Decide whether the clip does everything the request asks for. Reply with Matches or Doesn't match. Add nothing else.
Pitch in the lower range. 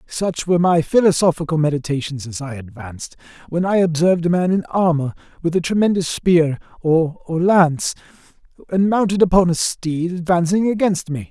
Doesn't match